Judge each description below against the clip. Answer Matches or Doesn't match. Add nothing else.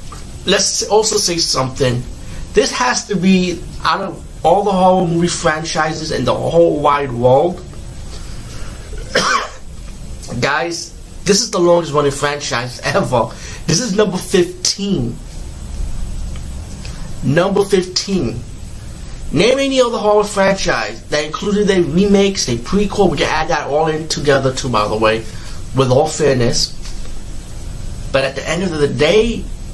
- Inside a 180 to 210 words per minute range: Doesn't match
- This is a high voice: Doesn't match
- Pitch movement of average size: Doesn't match